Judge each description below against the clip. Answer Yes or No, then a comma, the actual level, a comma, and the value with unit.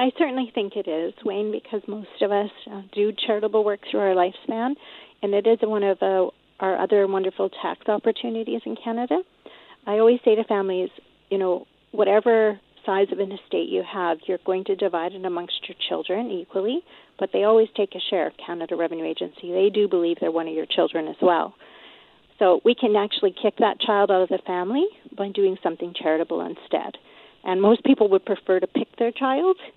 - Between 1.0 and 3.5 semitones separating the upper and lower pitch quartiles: Yes, average, 3.2 semitones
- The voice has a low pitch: No, high, 200 Hz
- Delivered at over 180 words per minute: Yes, average, 200 wpm